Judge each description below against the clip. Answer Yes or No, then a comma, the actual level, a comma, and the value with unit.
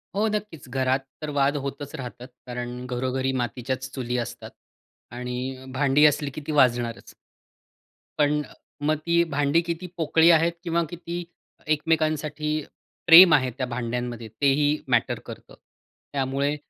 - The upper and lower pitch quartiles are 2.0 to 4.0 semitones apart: Yes, average, 3.6 semitones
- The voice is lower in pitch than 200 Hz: Yes, medium, 140 Hz